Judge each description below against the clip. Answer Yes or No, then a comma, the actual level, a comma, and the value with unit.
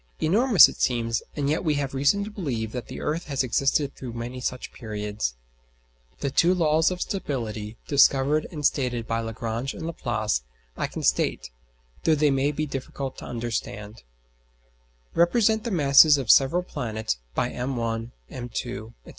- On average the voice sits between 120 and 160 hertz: Yes, low, 135 Hz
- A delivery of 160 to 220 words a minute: Yes, average, 165 wpm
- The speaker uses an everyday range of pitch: Yes, average, 5.0 semitones